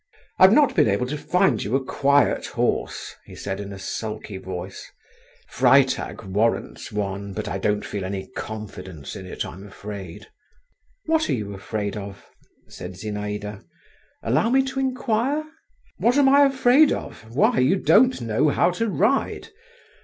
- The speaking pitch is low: Yes, low, 110 Hz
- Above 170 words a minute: No, average, 160 wpm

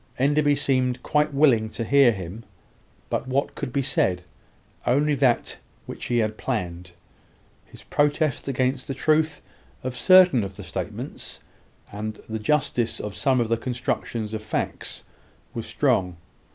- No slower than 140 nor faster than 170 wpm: Yes, average, 145 wpm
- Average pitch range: Yes, average, 4.5 semitones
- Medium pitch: No, low, 125 Hz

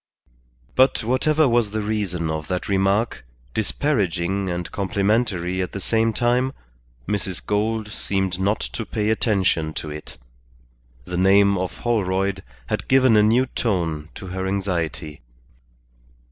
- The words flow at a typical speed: No, slow, 130 wpm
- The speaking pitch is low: Yes, low, 100 Hz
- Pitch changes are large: No, average, 3.4 semitones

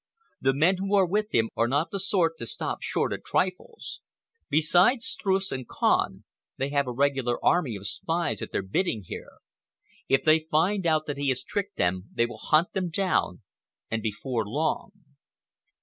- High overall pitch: No, medium, 155 Hz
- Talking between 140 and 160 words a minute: No, average, 180 wpm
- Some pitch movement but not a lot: No, wide, 7.2 semitones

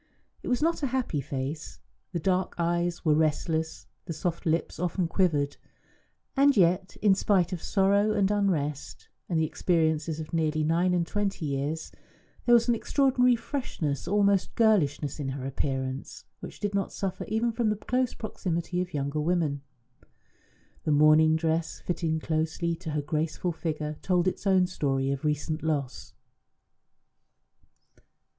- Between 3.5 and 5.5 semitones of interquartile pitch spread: Yes, average, 4.2 semitones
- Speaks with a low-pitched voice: No, medium, 170 Hz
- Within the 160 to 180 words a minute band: No, average, 150 wpm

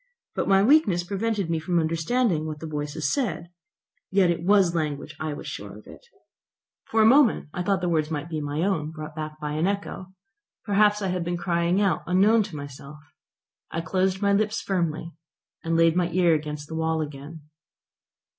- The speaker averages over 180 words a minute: Yes, average, 190 wpm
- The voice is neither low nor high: Yes, medium, 170 Hz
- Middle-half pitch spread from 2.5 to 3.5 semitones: No, average, 4.0 semitones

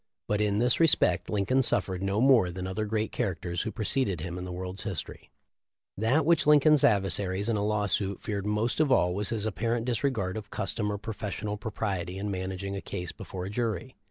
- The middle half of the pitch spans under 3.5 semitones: Yes, average, 3.1 semitones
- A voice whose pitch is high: No, low, 105 Hz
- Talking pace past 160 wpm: Yes, average, 195 wpm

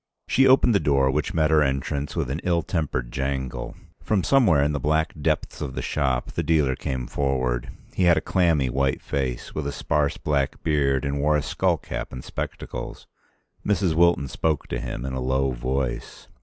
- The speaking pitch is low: Yes, very low, 70 Hz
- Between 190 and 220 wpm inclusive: Yes, average, 195 wpm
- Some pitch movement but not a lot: Yes, average, 3.1 semitones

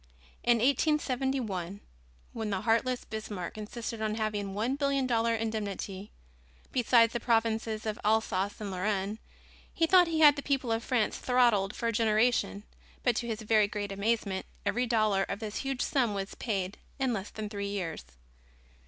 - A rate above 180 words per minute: No, average, 165 wpm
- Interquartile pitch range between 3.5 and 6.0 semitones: No, average, 3.1 semitones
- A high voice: Yes, high, 220 Hz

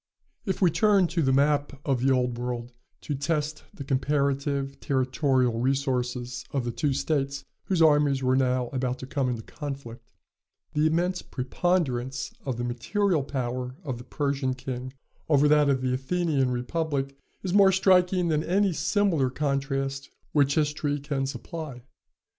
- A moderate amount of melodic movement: Yes, average, 3.1 semitones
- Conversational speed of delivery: Yes, average, 155 wpm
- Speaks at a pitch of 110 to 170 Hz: Yes, medium, 140 Hz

